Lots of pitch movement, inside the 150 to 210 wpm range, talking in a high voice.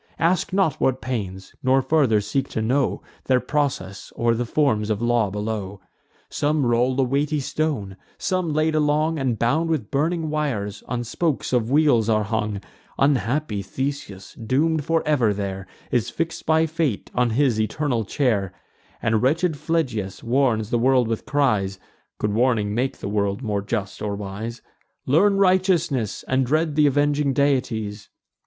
No: wide, 5.7 semitones; average, 155 wpm; low, 130 Hz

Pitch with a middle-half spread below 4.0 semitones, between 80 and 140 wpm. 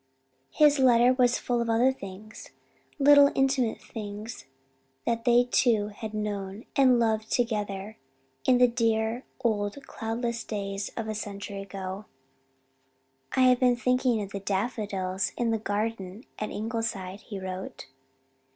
Yes: average, 3.2 semitones; slow, 135 wpm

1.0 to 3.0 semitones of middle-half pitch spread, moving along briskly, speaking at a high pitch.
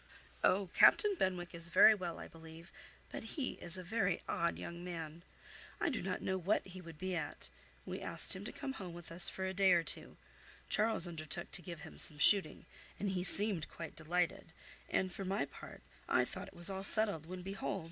No: narrow, 2.6 semitones; fast, 210 wpm; medium, 180 Hz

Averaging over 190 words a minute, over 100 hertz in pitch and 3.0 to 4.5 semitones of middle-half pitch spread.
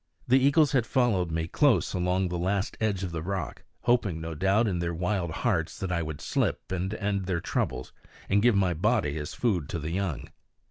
No: average, 200 wpm; very low, 95 Hz; average, 3.8 semitones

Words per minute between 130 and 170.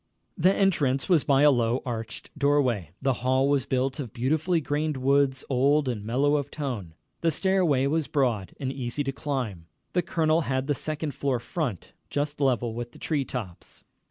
No: average, 180 wpm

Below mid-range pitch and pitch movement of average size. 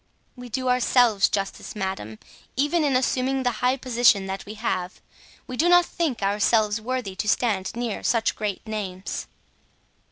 No: high, 230 Hz; average, 4.2 semitones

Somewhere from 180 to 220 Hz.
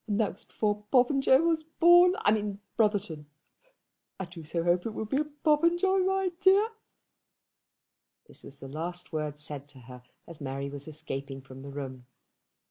Yes: high, 190 Hz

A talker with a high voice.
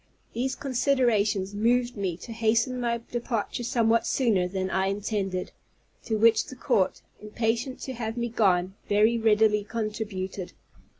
Yes: high, 220 Hz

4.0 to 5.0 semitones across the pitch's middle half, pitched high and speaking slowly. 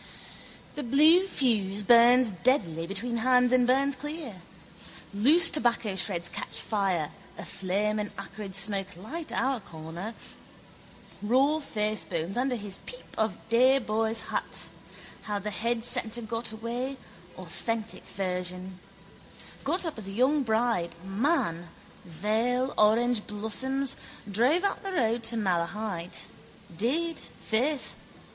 Yes: average, 4.7 semitones; high, 225 Hz; slow, 120 wpm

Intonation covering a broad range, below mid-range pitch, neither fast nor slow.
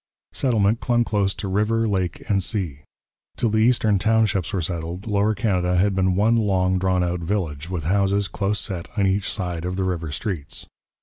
No: average, 2.8 semitones; very low, 95 Hz; average, 185 wpm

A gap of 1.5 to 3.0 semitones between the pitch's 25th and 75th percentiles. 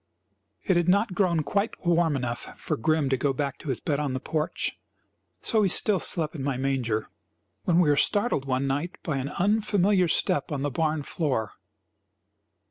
No: average, 4.8 semitones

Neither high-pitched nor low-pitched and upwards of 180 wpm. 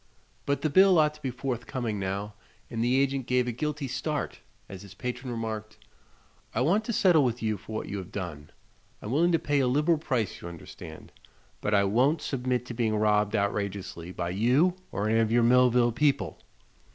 No: low, 120 Hz; average, 195 wpm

